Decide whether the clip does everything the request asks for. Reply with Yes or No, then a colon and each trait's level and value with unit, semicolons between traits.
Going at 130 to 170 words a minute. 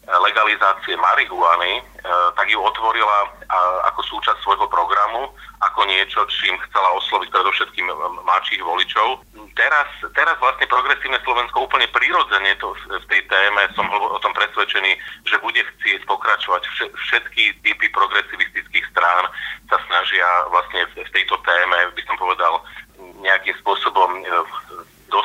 No: average, 120 wpm